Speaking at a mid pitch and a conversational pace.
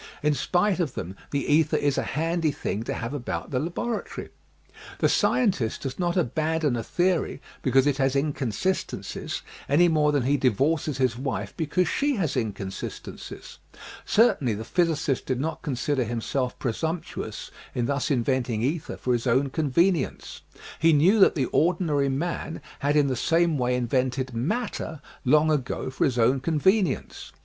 Yes: medium, 145 Hz; average, 170 wpm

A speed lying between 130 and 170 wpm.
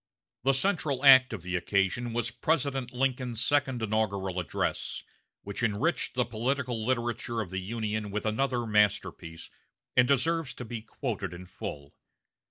Yes: average, 145 wpm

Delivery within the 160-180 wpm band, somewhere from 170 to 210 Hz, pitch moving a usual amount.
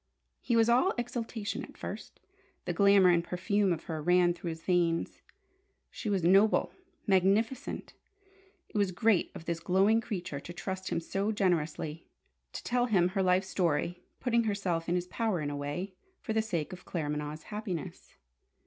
Yes: average, 165 wpm; medium, 185 Hz; average, 3.6 semitones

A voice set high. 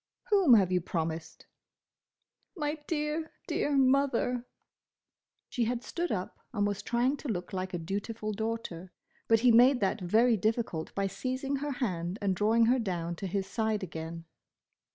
Yes: high, 220 Hz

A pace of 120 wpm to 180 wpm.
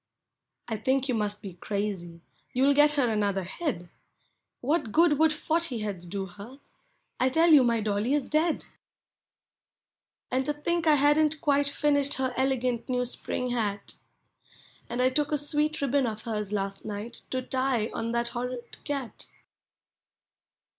Yes: average, 155 wpm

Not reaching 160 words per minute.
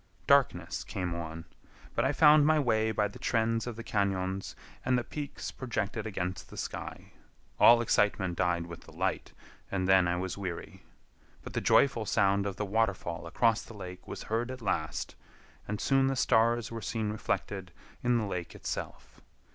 No: average, 175 wpm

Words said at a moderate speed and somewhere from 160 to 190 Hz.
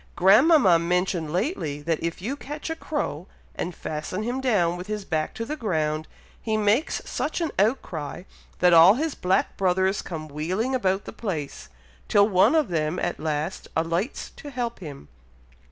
Yes: average, 170 wpm; medium, 185 Hz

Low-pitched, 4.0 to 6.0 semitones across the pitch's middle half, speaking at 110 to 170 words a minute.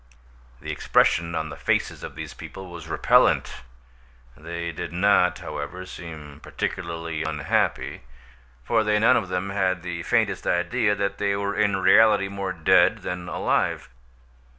No: very low, 90 Hz; average, 3.2 semitones; average, 145 wpm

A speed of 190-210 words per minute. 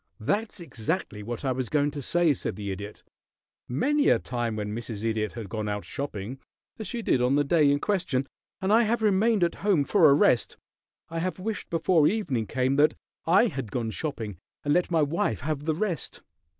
Yes: average, 200 wpm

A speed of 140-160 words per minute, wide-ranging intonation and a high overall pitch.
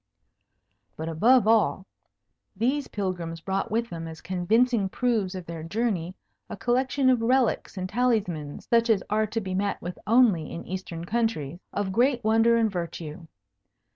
No: average, 155 wpm; average, 5.0 semitones; high, 205 Hz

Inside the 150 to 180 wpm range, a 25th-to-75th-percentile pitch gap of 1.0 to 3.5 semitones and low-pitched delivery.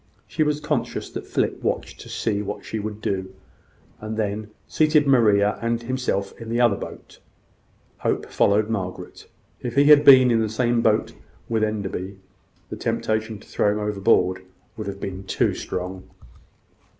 Yes: average, 160 wpm; average, 2.8 semitones; low, 110 Hz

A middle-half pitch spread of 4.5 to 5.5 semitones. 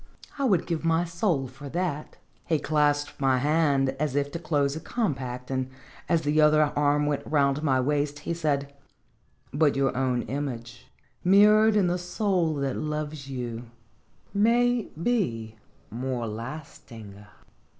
No: average, 3.8 semitones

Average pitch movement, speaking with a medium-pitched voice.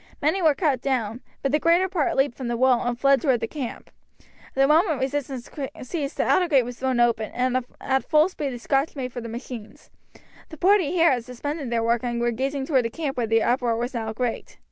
No: average, 3.4 semitones; very high, 260 Hz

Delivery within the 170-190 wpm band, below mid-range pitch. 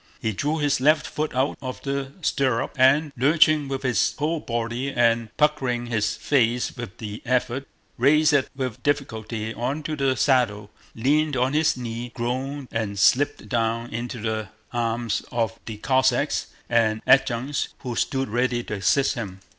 No: average, 155 wpm; low, 125 Hz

